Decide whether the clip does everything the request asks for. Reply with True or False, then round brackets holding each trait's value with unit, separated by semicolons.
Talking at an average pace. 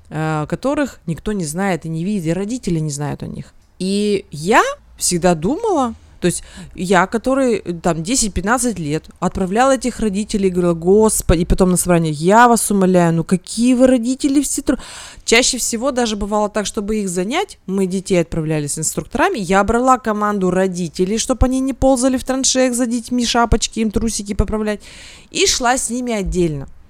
False (170 wpm)